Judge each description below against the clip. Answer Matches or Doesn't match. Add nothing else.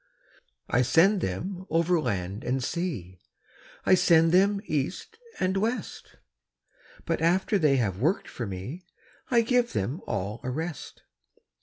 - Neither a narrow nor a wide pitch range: Doesn't match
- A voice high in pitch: Doesn't match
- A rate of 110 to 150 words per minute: Matches